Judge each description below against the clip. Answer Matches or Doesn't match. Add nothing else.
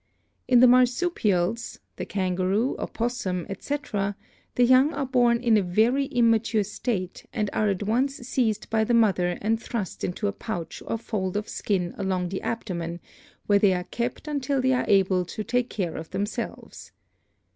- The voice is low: Doesn't match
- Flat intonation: Doesn't match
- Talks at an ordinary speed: Matches